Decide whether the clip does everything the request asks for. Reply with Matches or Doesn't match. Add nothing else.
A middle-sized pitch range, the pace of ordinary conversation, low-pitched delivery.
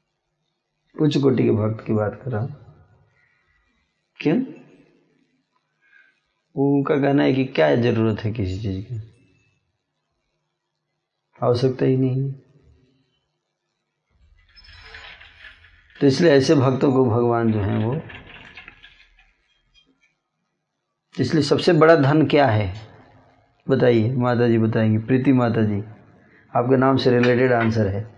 Doesn't match